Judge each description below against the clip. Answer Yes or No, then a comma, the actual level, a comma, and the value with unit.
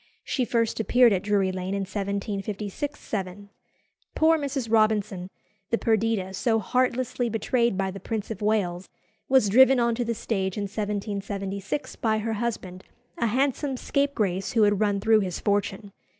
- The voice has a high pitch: Yes, high, 215 Hz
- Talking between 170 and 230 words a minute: No, average, 155 wpm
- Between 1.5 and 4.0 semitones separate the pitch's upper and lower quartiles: Yes, average, 3.1 semitones